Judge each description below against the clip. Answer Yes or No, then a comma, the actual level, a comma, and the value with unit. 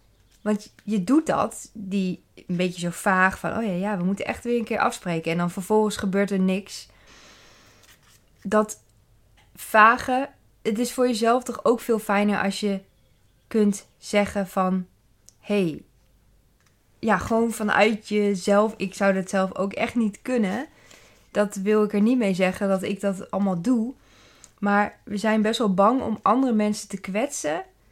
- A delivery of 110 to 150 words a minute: No, average, 165 wpm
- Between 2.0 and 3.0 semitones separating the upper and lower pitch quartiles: Yes, narrow, 2.6 semitones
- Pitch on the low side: No, high, 205 Hz